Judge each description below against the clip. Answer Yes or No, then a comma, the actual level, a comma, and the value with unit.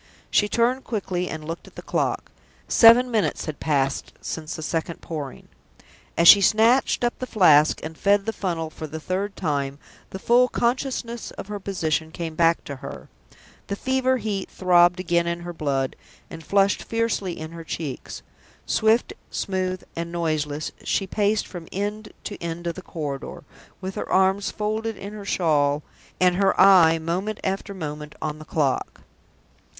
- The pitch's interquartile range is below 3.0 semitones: No, average, 4.5 semitones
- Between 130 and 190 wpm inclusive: Yes, average, 165 wpm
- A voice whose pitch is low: No, medium, 180 Hz